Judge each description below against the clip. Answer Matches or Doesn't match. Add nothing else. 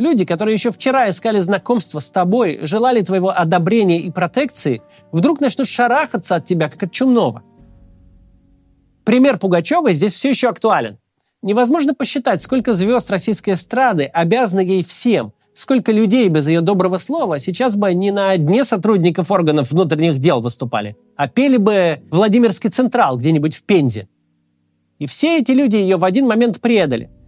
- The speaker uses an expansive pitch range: Matches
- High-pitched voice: Matches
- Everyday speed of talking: Matches